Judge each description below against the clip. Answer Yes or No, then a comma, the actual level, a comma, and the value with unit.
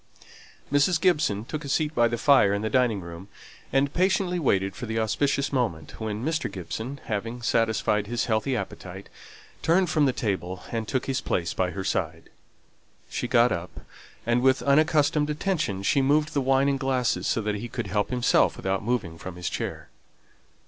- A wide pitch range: Yes, wide, 5.8 semitones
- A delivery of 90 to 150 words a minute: No, average, 175 wpm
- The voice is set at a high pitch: No, low, 120 Hz